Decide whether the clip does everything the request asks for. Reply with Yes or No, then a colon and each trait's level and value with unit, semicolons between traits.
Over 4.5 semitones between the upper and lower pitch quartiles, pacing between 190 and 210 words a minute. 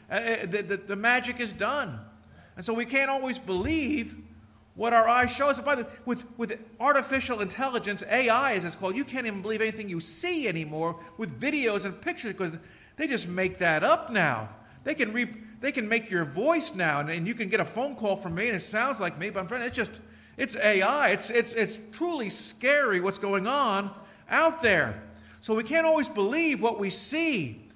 Yes: average, 5.1 semitones; fast, 205 wpm